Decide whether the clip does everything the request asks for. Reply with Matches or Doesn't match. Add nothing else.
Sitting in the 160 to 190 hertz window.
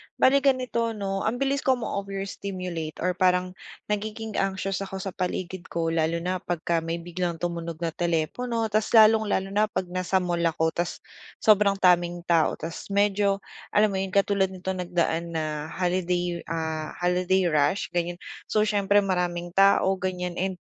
Matches